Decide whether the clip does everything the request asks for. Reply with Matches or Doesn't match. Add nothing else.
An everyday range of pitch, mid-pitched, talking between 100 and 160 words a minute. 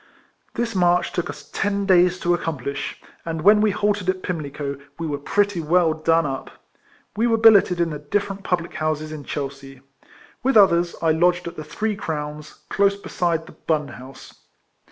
Doesn't match